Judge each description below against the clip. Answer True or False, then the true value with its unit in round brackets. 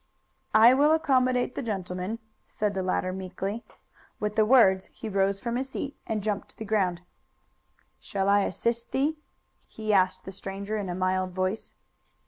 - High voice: True (205 Hz)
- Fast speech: False (165 wpm)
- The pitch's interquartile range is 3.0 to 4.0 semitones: True (3.7 semitones)